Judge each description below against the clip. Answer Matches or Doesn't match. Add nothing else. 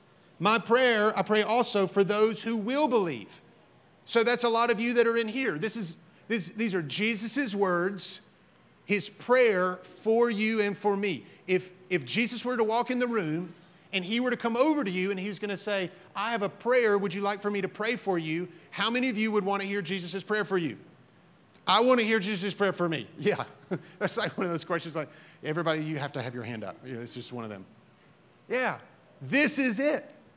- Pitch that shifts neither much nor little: Matches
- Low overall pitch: Doesn't match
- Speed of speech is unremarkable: Doesn't match